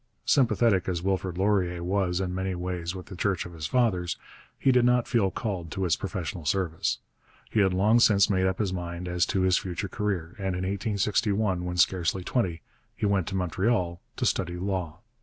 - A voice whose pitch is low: Yes, very low, 95 Hz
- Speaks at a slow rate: No, average, 195 wpm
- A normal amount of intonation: No, narrow, 2.3 semitones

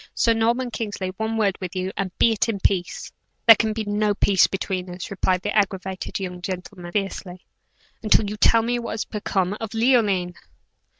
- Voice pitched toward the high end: Yes, high, 200 Hz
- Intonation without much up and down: No, average, 3.1 semitones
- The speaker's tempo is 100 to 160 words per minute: No, average, 185 wpm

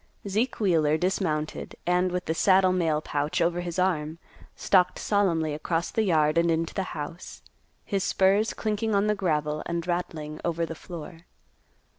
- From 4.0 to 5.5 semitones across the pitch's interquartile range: No, average, 3.1 semitones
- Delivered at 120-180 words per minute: Yes, average, 160 wpm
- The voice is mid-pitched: Yes, medium, 175 Hz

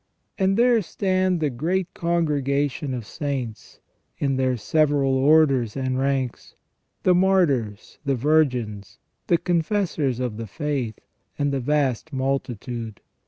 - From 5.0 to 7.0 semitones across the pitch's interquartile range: No, average, 4.1 semitones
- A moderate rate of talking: No, slow, 120 wpm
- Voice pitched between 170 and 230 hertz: No, medium, 140 Hz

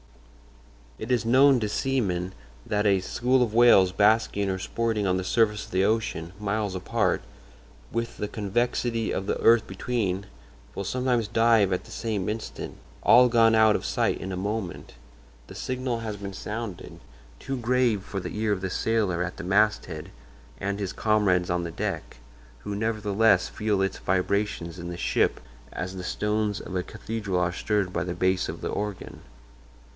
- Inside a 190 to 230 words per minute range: No, average, 170 wpm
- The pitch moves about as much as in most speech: Yes, average, 3.4 semitones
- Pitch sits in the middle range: No, low, 105 Hz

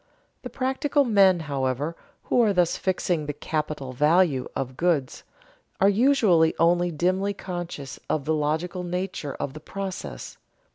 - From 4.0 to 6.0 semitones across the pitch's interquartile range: Yes, average, 4.4 semitones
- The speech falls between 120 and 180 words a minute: Yes, average, 140 wpm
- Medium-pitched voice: Yes, medium, 175 Hz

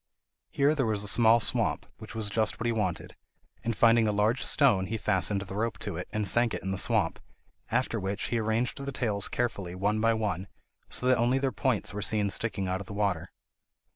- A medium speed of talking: No, fast, 220 wpm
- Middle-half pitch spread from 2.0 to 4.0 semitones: Yes, average, 2.8 semitones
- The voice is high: No, low, 110 Hz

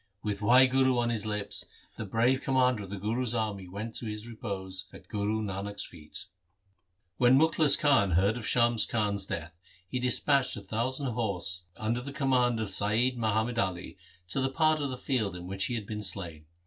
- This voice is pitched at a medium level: No, low, 110 Hz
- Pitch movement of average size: Yes, average, 4.1 semitones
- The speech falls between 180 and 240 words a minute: Yes, average, 185 wpm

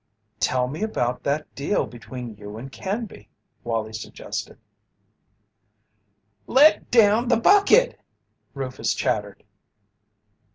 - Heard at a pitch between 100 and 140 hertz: Yes, low, 135 Hz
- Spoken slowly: Yes, slow, 95 wpm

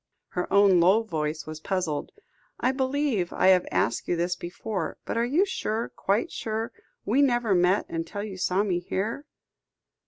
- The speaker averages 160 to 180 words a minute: Yes, average, 165 wpm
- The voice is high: Yes, high, 200 Hz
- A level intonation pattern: No, average, 4.6 semitones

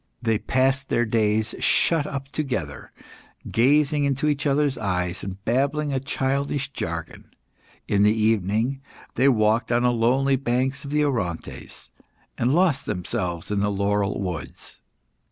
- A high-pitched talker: No, low, 125 Hz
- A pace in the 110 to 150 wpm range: Yes, average, 140 wpm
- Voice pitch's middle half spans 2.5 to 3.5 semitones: No, average, 5.0 semitones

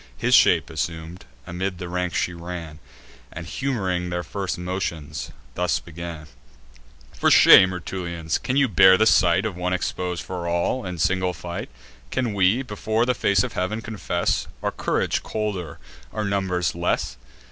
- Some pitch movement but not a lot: No, narrow, 2.3 semitones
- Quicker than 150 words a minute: Yes, average, 160 wpm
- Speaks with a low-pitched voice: Yes, very low, 90 Hz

